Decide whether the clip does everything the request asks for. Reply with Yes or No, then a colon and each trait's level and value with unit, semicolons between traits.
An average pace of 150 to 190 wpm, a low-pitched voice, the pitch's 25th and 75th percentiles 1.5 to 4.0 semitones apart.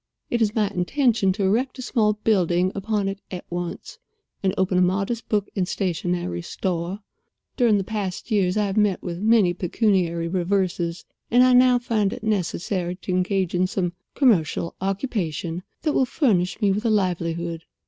No: average, 170 wpm; high, 195 Hz; average, 3.4 semitones